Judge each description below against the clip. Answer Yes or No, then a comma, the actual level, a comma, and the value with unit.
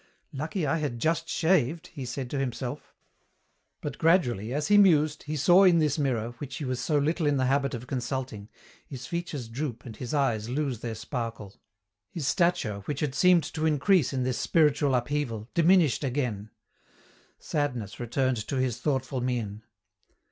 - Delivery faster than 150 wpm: Yes, average, 170 wpm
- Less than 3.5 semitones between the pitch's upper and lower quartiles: No, average, 4.1 semitones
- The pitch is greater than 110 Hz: Yes, low, 135 Hz